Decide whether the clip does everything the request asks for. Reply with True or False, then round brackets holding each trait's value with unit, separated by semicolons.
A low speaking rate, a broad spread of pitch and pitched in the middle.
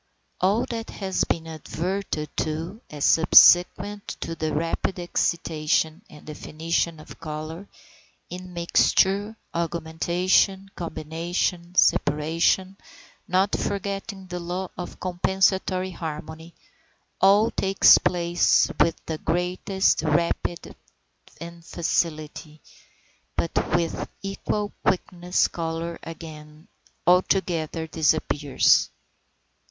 False (90 wpm; 2.7 semitones; 170 Hz)